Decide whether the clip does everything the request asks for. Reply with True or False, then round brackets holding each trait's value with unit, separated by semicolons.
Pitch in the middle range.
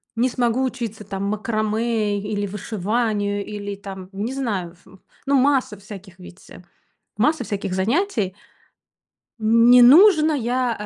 False (215 Hz)